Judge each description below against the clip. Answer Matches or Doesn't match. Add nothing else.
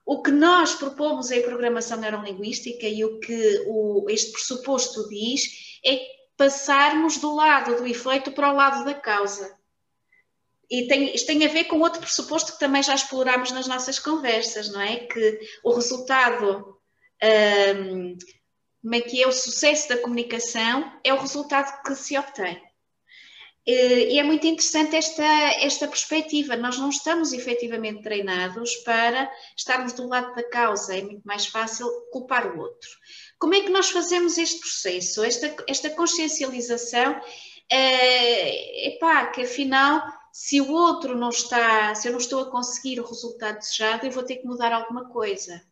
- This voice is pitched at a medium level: Doesn't match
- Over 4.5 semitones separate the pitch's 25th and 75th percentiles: Doesn't match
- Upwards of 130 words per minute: Matches